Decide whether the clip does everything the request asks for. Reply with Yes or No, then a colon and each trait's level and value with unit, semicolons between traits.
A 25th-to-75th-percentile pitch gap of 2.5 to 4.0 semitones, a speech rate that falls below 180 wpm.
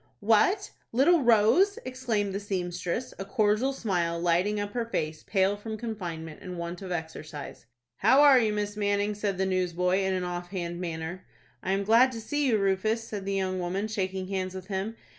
No: average, 3.4 semitones; average, 190 wpm